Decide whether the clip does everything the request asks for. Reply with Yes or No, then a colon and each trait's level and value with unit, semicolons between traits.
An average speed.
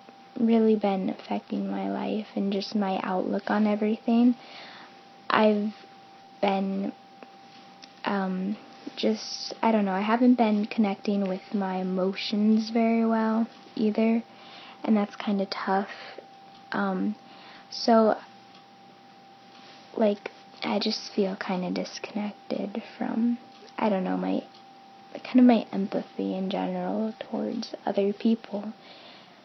No: slow, 115 wpm